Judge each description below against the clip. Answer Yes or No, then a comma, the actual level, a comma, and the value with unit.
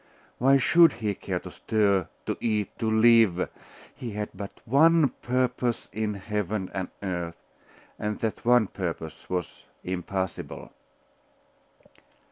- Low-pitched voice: Yes, low, 105 Hz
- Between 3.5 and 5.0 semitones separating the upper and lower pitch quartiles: Yes, average, 4.0 semitones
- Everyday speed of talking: No, slow, 120 wpm